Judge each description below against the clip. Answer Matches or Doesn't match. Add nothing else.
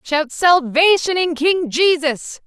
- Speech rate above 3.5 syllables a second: Doesn't match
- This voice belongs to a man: Doesn't match